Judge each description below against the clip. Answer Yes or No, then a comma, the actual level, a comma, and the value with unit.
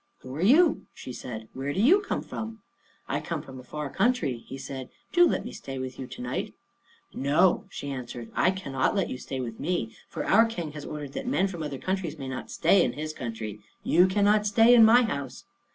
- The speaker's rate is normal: No, fast, 220 wpm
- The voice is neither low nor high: Yes, medium, 150 Hz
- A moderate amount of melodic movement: No, wide, 7.7 semitones